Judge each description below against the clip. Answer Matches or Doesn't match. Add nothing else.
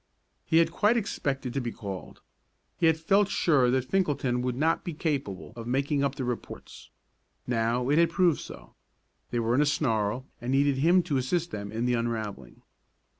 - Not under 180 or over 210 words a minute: Matches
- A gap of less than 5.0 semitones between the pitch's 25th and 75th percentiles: Doesn't match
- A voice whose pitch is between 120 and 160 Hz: Matches